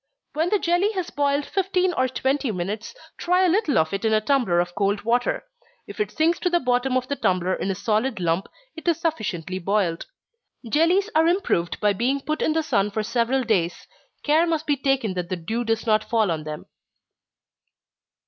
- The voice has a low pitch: No, high, 245 Hz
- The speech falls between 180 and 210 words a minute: Yes, average, 200 wpm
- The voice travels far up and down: Yes, wide, 8.3 semitones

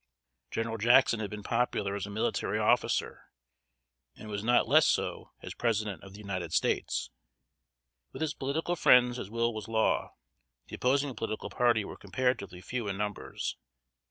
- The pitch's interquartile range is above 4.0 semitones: No, average, 3.3 semitones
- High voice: No, low, 110 Hz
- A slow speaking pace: No, average, 155 wpm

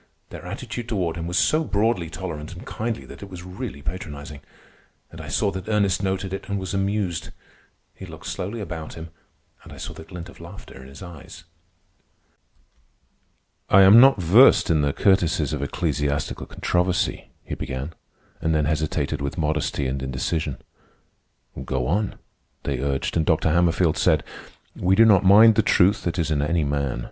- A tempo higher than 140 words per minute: Yes, average, 175 wpm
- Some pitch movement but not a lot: Yes, average, 4.4 semitones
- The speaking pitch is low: Yes, very low, 85 Hz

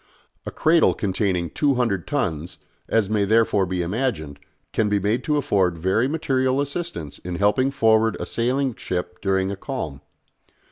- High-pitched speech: No, low, 105 Hz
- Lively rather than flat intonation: Yes, wide, 6.2 semitones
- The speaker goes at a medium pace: Yes, average, 150 wpm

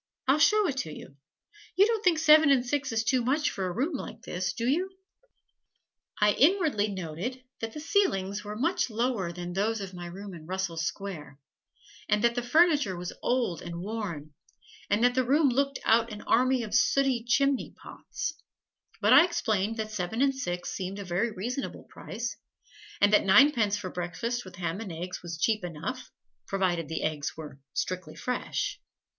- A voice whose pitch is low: No, high, 215 Hz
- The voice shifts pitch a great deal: Yes, wide, 6.3 semitones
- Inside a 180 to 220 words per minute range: Yes, average, 185 wpm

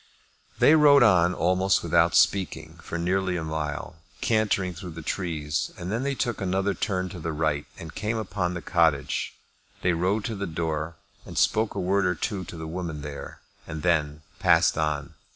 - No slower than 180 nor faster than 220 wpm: Yes, average, 185 wpm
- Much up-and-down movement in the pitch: No, average, 3.6 semitones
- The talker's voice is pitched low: Yes, very low, 90 Hz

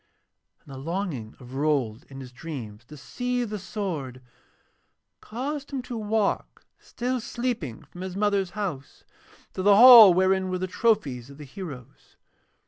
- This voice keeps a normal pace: Yes, average, 150 wpm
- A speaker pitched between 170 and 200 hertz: Yes, medium, 185 Hz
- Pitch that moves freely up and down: Yes, wide, 7.9 semitones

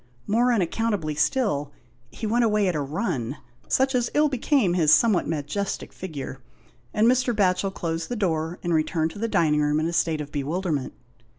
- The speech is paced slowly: No, average, 180 wpm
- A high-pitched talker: No, medium, 175 Hz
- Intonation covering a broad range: Yes, wide, 6.5 semitones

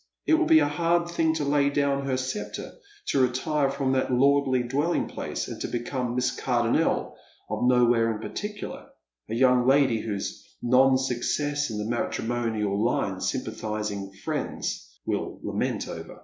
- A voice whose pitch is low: Yes, low, 130 Hz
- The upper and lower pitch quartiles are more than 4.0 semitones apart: No, average, 3.3 semitones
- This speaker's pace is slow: No, average, 155 wpm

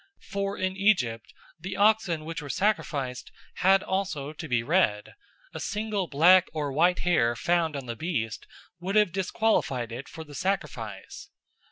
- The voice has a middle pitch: Yes, medium, 165 Hz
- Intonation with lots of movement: Yes, wide, 6.2 semitones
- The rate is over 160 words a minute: No, average, 155 wpm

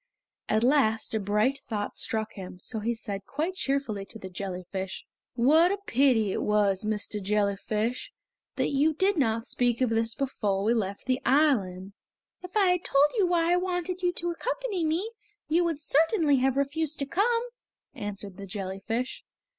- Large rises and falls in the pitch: Yes, wide, 7.6 semitones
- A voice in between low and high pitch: No, very high, 250 Hz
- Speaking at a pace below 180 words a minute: Yes, average, 170 wpm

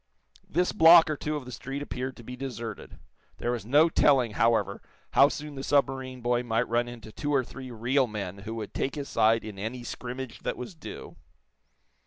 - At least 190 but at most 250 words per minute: Yes, average, 200 wpm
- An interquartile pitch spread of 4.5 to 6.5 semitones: No, average, 3.3 semitones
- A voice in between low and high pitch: No, low, 125 Hz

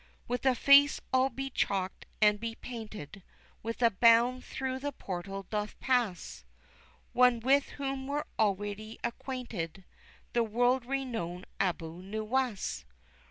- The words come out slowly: Yes, slow, 125 wpm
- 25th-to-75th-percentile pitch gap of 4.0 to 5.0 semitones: Yes, average, 4.4 semitones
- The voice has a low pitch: No, high, 230 Hz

